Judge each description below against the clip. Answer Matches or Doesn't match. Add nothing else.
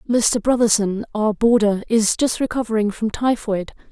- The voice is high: Matches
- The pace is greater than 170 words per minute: Doesn't match